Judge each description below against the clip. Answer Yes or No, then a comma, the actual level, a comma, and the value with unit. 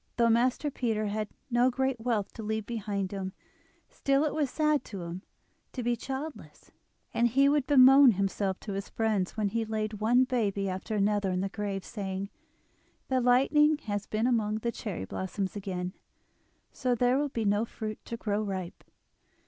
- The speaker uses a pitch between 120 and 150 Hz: No, high, 220 Hz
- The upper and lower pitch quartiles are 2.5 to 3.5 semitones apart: No, average, 4.0 semitones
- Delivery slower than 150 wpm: No, average, 175 wpm